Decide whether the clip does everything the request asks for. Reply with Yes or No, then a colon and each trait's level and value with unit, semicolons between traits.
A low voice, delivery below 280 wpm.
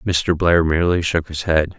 Yes: very low, 85 Hz; average, 200 wpm